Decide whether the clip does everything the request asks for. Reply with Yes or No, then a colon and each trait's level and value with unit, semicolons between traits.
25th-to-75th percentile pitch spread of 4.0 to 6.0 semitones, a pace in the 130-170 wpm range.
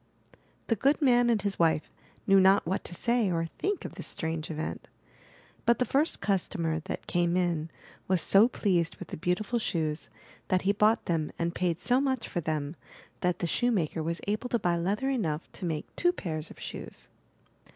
No: wide, 5.5 semitones; average, 190 wpm